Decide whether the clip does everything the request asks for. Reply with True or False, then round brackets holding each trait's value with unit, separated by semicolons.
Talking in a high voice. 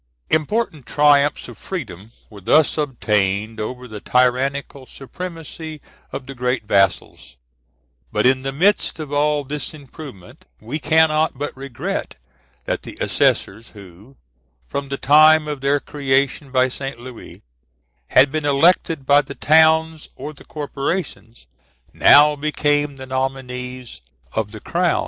False (140 Hz)